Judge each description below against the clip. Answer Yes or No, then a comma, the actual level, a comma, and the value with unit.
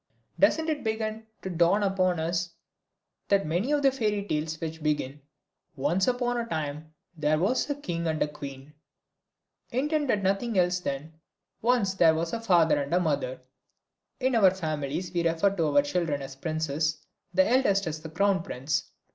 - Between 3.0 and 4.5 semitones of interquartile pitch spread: No, average, 4.9 semitones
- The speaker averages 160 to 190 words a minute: Yes, average, 165 wpm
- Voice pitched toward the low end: No, medium, 170 Hz